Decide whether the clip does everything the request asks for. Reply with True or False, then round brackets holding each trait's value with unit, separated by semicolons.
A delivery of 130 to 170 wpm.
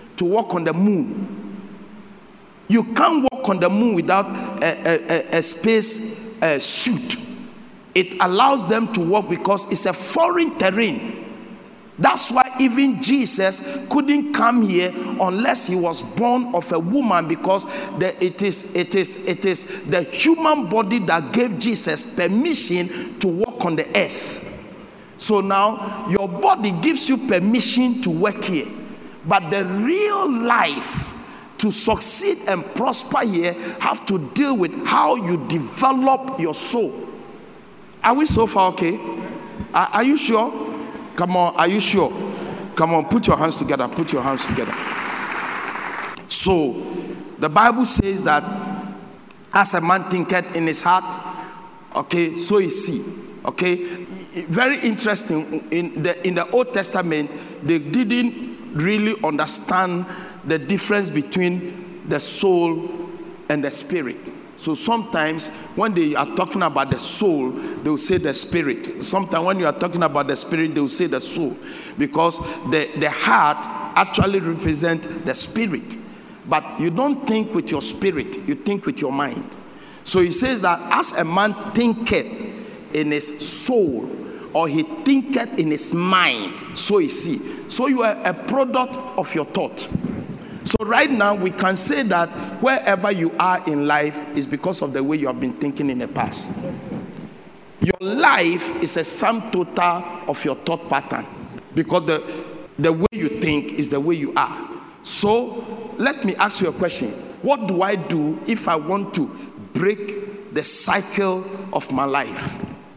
True (155 wpm)